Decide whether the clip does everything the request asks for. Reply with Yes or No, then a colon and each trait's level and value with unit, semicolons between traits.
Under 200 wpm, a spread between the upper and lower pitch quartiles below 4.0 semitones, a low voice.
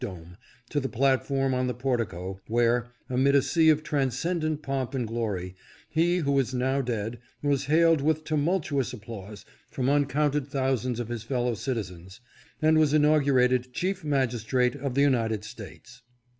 Yes: average, 155 wpm; average, 3.6 semitones; low, 130 Hz